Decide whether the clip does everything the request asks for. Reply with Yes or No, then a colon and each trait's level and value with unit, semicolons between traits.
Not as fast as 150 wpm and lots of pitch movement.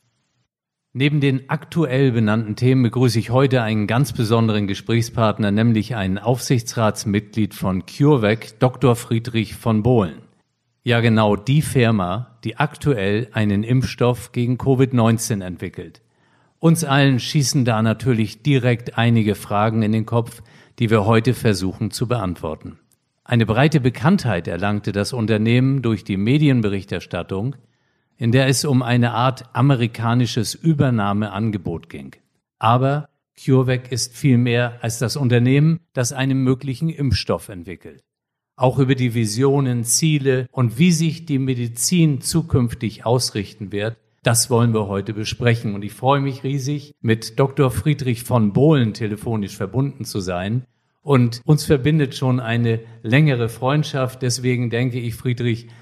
No: average, 130 wpm; average, 3.3 semitones